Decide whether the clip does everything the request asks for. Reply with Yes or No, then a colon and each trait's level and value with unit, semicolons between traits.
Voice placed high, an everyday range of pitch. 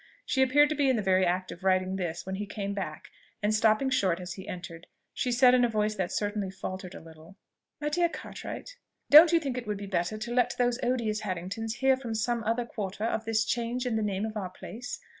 Yes: high, 215 Hz; average, 4.5 semitones